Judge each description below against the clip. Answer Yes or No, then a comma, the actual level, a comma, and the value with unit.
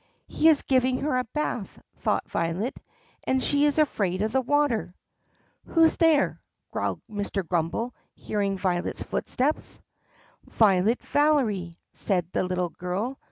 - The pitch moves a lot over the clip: Yes, wide, 7.5 semitones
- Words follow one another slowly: Yes, slow, 130 wpm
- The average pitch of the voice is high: Yes, high, 225 Hz